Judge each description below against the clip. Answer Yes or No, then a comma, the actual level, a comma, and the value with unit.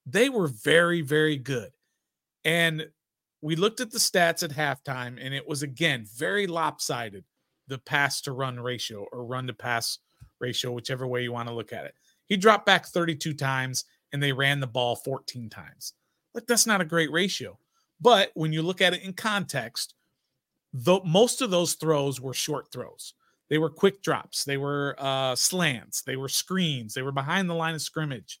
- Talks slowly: No, average, 190 wpm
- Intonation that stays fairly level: No, average, 4.7 semitones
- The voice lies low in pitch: No, medium, 150 Hz